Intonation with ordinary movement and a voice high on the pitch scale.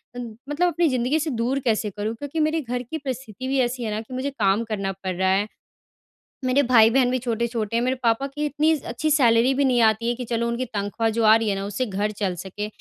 Yes: average, 3.6 semitones; high, 235 Hz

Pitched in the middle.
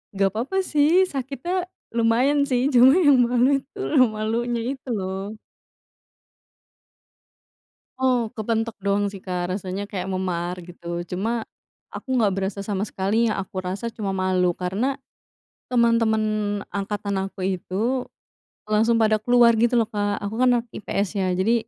No: high, 215 Hz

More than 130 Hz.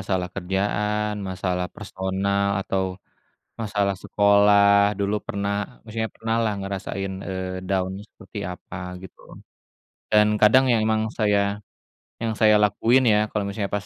No: low, 100 Hz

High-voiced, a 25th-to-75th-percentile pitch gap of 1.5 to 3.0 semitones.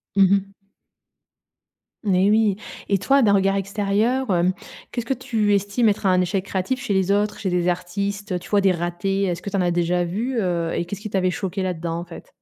Yes: high, 195 Hz; narrow, 2.4 semitones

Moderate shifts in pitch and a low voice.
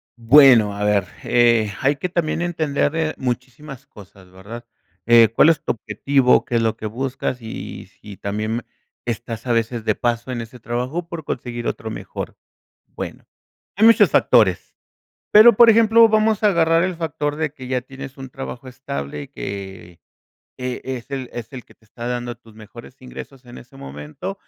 Yes: average, 4.7 semitones; low, 125 Hz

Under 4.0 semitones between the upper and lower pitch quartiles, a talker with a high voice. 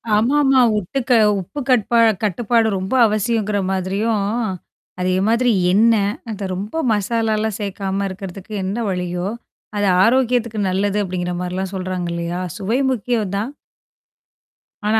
Yes: average, 3.3 semitones; high, 205 Hz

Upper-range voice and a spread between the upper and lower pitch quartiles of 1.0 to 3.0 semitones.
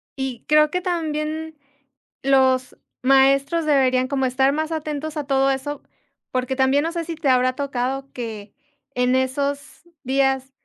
Yes: very high, 275 Hz; average, 2.7 semitones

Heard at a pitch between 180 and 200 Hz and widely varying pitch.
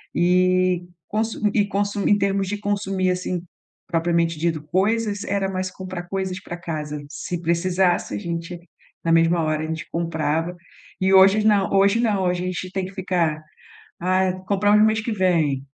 No: medium, 185 Hz; average, 2.7 semitones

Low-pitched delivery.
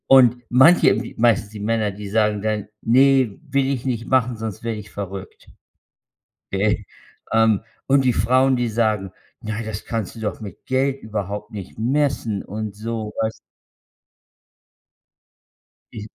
Yes: low, 110 Hz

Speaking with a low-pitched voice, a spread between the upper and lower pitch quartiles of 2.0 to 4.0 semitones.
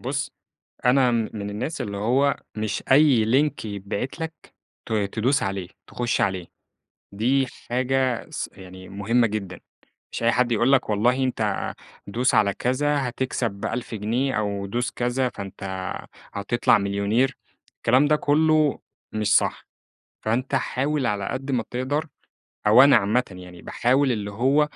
No: low, 120 Hz; average, 4.5 semitones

